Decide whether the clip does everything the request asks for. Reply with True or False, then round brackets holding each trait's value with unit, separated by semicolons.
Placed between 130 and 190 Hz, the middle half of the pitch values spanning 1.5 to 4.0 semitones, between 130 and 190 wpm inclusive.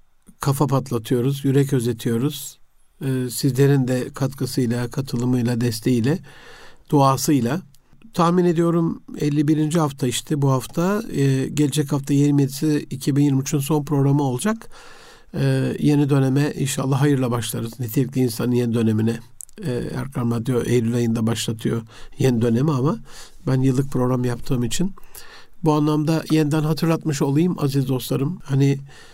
False (140 Hz; 3.4 semitones; 120 wpm)